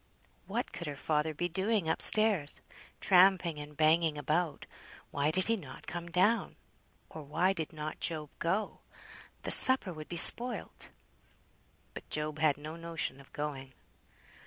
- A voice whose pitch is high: No, medium, 160 Hz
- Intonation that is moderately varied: Yes, average, 3.4 semitones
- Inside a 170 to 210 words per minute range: No, average, 150 wpm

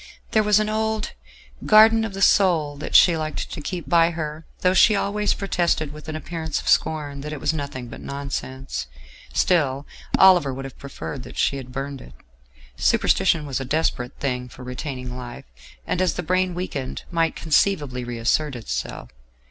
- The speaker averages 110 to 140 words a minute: No, average, 175 wpm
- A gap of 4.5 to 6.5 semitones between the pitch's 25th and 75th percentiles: Yes, average, 5.3 semitones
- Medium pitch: Yes, medium, 150 Hz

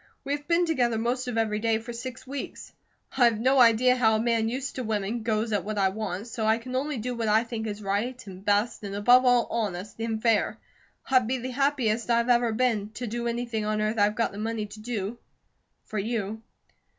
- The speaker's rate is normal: No, fast, 225 wpm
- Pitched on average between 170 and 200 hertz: No, high, 230 Hz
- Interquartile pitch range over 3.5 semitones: No, narrow, 2.4 semitones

